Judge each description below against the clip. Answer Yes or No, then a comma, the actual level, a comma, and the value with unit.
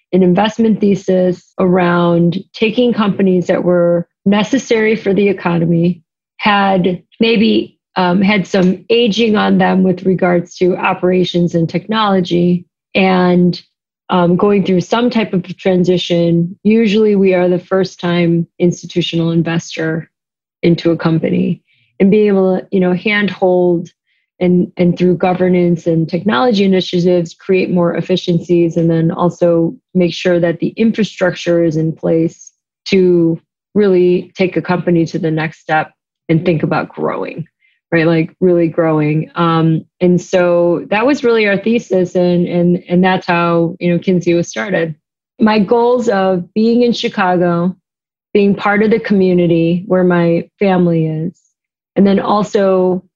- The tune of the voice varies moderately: No, narrow, 2.2 semitones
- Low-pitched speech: No, medium, 180 Hz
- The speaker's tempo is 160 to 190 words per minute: No, average, 140 wpm